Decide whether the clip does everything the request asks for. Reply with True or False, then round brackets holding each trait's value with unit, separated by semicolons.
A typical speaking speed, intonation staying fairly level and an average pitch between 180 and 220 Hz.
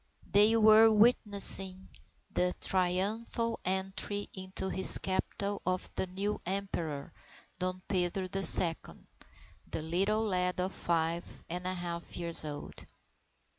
False (120 wpm; 2.3 semitones; 185 Hz)